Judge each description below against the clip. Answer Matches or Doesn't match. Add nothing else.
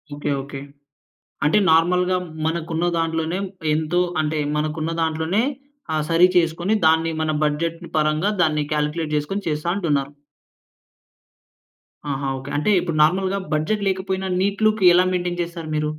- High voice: Doesn't match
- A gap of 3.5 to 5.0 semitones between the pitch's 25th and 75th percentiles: Doesn't match